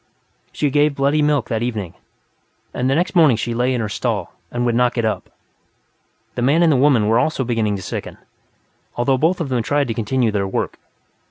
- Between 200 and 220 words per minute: Yes, fast, 205 wpm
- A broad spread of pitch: No, average, 4.1 semitones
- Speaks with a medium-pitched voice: No, low, 125 Hz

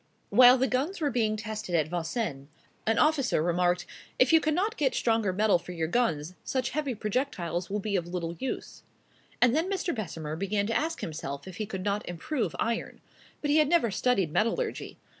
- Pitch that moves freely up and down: Yes, wide, 7.0 semitones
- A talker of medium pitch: No, high, 215 Hz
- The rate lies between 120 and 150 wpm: No, average, 190 wpm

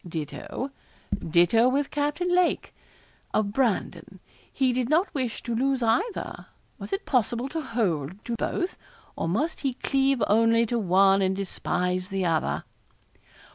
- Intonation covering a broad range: Yes, wide, 6.1 semitones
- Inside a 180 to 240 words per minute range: No, average, 140 wpm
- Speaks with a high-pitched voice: Yes, high, 230 Hz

